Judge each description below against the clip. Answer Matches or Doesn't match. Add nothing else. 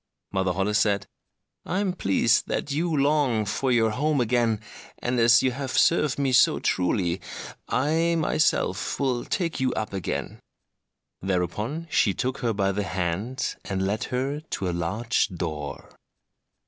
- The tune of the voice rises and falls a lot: Matches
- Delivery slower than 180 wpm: Matches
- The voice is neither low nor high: Doesn't match